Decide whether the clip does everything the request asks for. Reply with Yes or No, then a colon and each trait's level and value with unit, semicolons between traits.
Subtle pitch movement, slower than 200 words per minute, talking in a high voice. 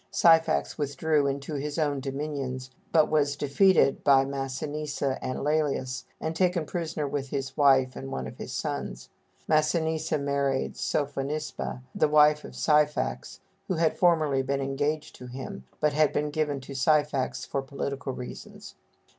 No: narrow, 2.2 semitones; average, 145 wpm; medium, 145 Hz